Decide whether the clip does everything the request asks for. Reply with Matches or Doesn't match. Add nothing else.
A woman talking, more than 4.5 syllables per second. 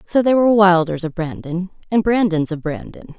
Matches